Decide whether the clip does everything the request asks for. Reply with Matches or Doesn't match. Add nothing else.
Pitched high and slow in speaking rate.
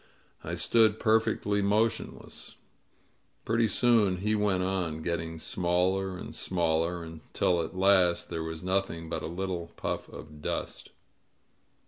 Doesn't match